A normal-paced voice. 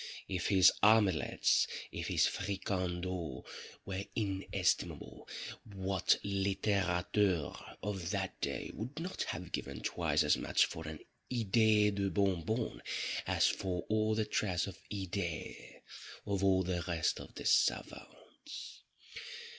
No: slow, 125 wpm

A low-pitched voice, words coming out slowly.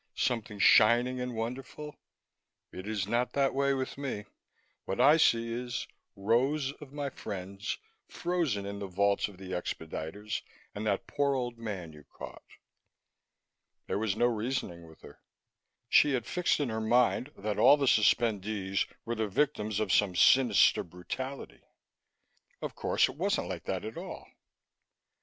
No: low, 110 Hz; average, 150 wpm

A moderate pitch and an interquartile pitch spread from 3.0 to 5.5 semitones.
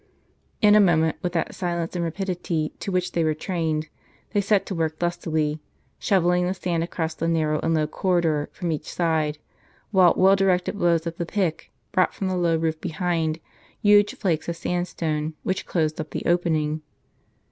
No: medium, 170 Hz; narrow, 2.4 semitones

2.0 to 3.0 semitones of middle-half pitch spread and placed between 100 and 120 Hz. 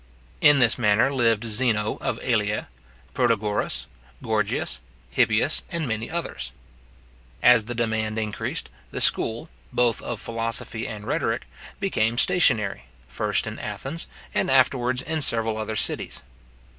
Yes: average, 2.7 semitones; low, 115 Hz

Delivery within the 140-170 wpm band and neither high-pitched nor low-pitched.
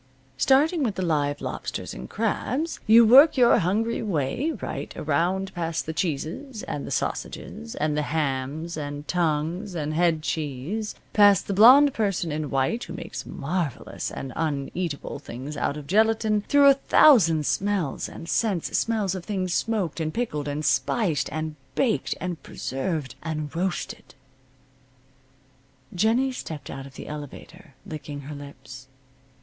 Yes: average, 145 wpm; medium, 165 Hz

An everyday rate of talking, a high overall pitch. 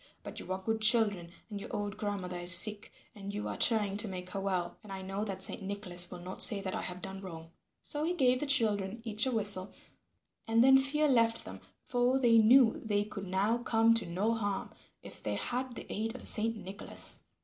No: fast, 220 wpm; high, 210 Hz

